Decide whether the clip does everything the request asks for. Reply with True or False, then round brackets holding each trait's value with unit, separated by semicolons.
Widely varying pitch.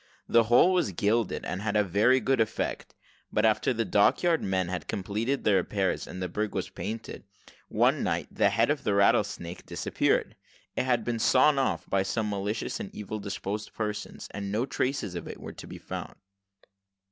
False (3.0 semitones)